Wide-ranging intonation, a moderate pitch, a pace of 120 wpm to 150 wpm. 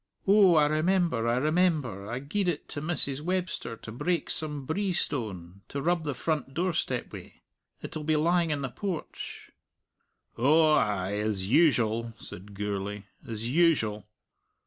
Yes: wide, 6.9 semitones; medium, 145 Hz; average, 145 wpm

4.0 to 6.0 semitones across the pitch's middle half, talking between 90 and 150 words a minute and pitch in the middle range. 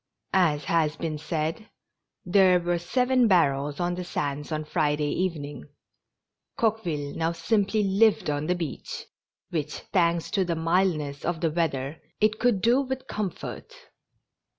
Yes: average, 4.5 semitones; average, 140 wpm; medium, 170 Hz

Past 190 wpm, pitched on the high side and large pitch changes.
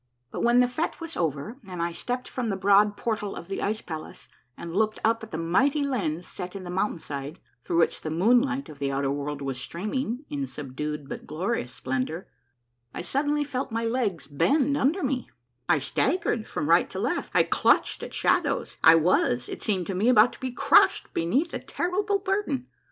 Yes: average, 200 wpm; high, 200 Hz; wide, 8.1 semitones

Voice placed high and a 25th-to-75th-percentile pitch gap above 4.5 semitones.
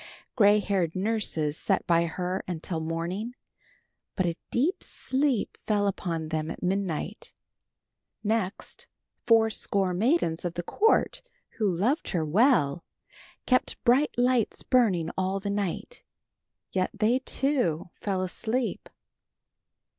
Yes: high, 195 Hz; average, 5.2 semitones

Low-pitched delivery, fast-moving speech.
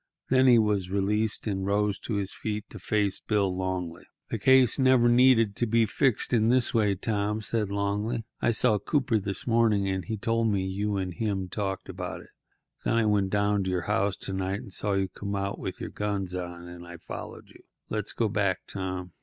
Yes: low, 100 Hz; fast, 210 wpm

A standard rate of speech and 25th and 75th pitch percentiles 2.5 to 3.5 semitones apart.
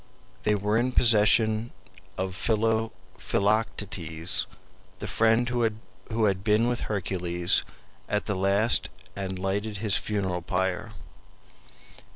No: slow, 105 wpm; average, 2.8 semitones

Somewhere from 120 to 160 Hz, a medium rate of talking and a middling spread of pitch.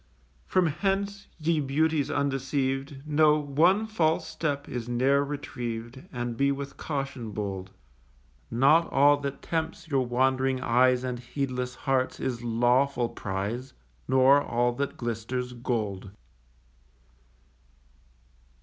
No: low, 135 Hz; slow, 115 wpm; average, 3.0 semitones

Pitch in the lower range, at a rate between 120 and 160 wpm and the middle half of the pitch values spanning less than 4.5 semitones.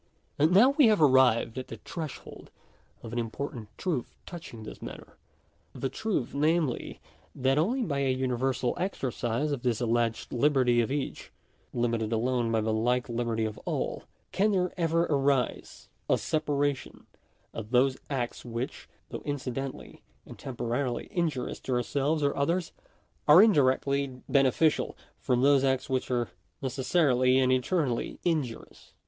Yes: low, 130 Hz; average, 145 wpm; average, 3.6 semitones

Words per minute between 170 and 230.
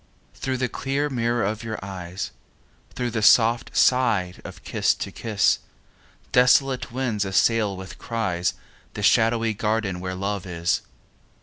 No: slow, 135 wpm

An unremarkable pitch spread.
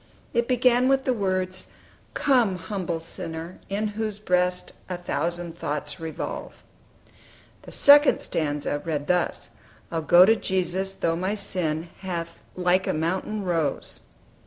Yes: average, 3.9 semitones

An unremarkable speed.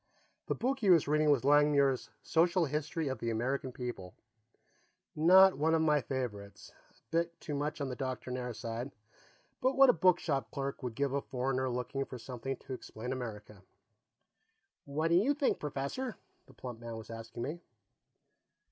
Yes: average, 165 wpm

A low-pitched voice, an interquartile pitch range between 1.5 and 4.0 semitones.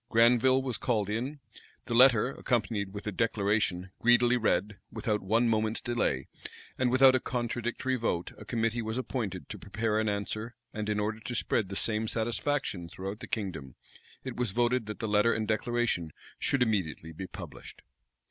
Yes: low, 110 Hz; average, 2.7 semitones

